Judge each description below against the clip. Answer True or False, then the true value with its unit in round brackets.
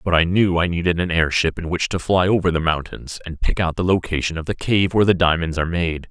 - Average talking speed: False (265 wpm)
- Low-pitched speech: True (85 Hz)